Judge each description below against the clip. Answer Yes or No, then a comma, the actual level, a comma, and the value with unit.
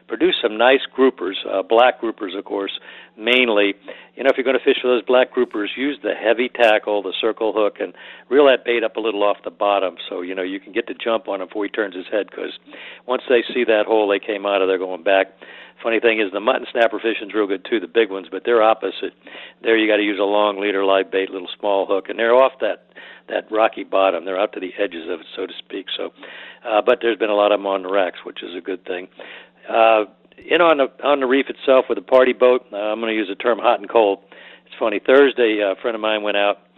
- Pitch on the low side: Yes, low, 110 Hz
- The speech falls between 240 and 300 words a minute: Yes, fast, 260 wpm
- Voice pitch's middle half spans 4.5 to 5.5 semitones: No, average, 3.7 semitones